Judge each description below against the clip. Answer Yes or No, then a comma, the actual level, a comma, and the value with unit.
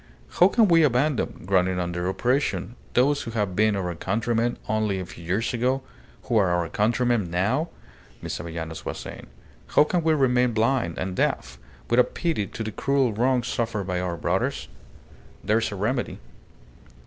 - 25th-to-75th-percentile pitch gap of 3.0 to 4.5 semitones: No, wide, 5.4 semitones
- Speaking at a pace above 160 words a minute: Yes, average, 170 wpm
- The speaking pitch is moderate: No, low, 110 Hz